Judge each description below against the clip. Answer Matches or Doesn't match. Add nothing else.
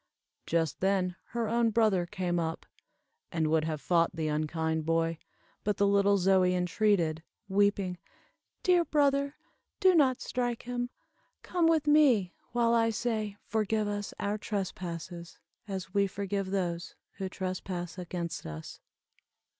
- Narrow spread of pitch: Doesn't match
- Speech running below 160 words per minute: Matches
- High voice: Matches